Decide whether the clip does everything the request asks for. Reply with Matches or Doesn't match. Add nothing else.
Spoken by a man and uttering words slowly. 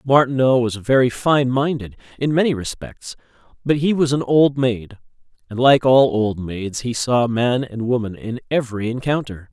Doesn't match